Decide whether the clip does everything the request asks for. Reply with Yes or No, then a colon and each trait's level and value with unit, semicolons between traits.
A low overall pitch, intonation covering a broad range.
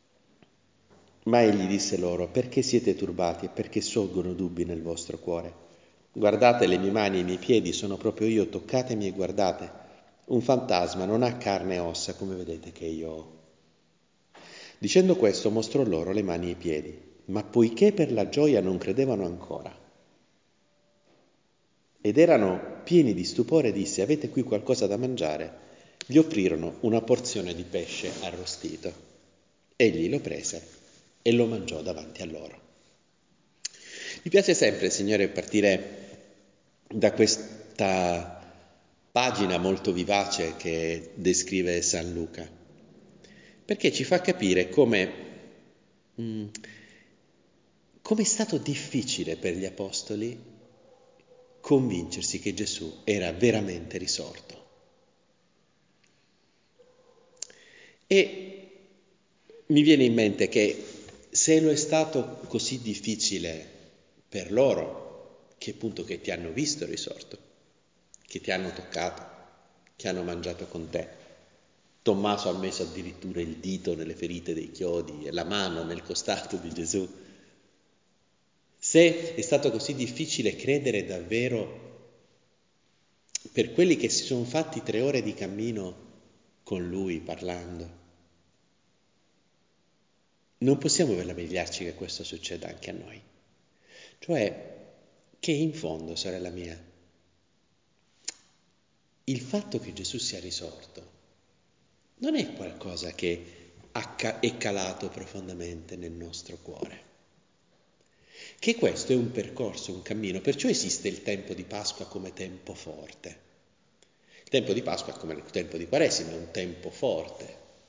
Yes: low, 100 Hz; wide, 6.3 semitones